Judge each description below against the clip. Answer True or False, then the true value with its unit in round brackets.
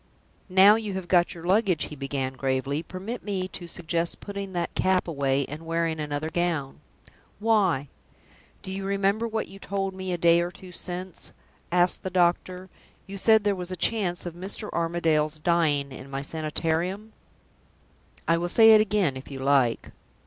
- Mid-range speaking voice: True (175 Hz)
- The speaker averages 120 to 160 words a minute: False (170 wpm)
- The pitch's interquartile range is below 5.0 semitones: True (3.8 semitones)